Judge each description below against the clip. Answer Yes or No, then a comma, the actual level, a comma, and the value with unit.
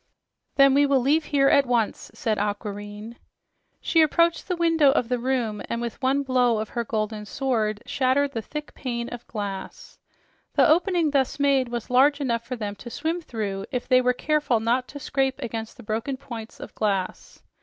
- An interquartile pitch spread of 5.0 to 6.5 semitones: No, average, 4.1 semitones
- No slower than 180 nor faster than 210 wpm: Yes, average, 185 wpm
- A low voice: No, very high, 250 Hz